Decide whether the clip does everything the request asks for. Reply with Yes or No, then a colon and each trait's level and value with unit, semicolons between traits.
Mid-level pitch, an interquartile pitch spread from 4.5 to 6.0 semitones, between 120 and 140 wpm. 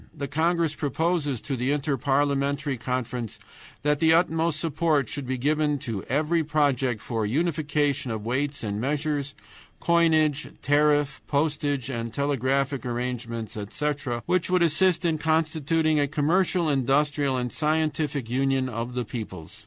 No: medium, 145 Hz; average, 3.5 semitones; slow, 135 wpm